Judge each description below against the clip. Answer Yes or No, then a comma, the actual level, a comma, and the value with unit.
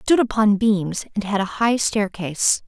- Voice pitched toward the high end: Yes, high, 210 Hz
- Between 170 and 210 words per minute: Yes, average, 200 wpm